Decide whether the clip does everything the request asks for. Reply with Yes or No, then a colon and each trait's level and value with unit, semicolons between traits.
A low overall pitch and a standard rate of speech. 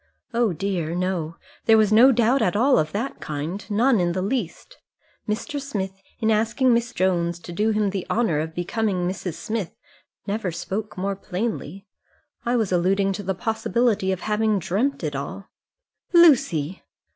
No: high, 200 Hz; average, 165 wpm